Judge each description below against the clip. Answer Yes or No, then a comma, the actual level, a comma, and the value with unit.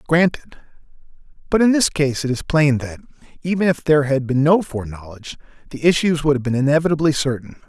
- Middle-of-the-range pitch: Yes, medium, 145 Hz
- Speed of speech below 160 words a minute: No, average, 180 wpm